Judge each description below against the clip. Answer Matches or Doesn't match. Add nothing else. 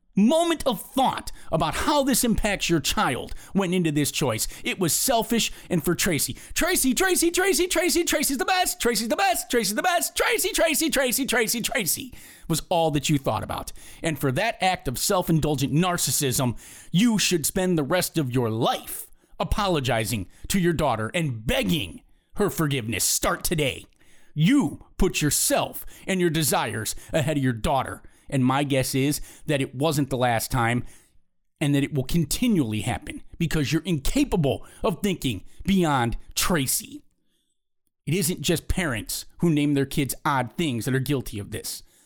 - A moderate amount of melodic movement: Doesn't match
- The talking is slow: Doesn't match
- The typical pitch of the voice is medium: Matches